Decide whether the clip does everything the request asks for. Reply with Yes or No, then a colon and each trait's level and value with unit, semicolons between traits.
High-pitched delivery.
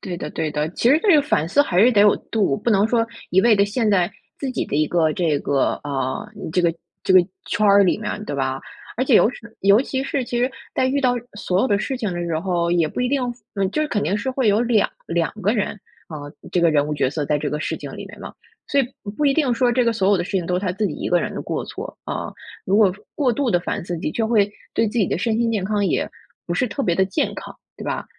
Yes: high, 205 Hz